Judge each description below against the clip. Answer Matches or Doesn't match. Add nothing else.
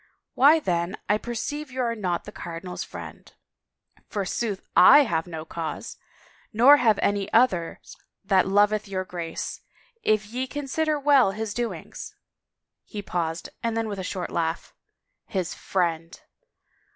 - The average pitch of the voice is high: Matches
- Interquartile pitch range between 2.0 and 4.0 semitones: Doesn't match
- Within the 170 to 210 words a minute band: Doesn't match